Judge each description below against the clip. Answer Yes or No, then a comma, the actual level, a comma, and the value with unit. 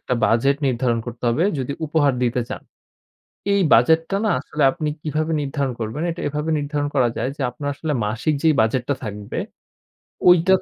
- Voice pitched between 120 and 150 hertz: Yes, medium, 140 Hz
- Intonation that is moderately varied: Yes, average, 4.3 semitones